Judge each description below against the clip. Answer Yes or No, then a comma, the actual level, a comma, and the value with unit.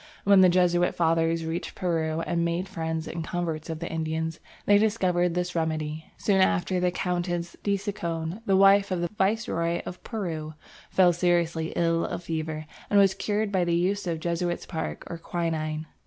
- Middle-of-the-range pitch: Yes, medium, 175 Hz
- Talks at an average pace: Yes, average, 170 wpm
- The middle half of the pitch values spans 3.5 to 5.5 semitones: No, narrow, 2.5 semitones